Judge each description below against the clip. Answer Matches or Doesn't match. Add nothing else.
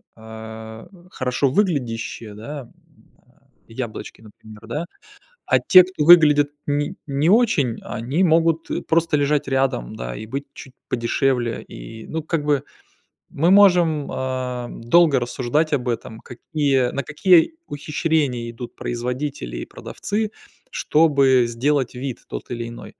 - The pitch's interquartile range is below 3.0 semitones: Doesn't match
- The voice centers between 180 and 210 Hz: Doesn't match